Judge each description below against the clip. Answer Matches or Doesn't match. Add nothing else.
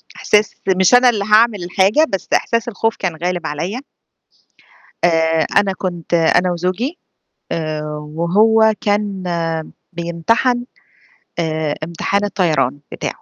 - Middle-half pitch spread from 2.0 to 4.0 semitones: Doesn't match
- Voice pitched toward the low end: Doesn't match